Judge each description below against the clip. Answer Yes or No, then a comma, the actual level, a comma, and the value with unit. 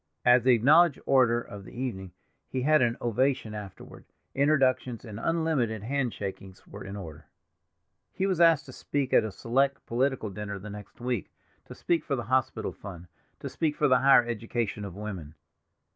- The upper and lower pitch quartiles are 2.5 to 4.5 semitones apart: No, average, 4.9 semitones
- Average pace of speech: Yes, average, 175 wpm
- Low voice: Yes, low, 120 Hz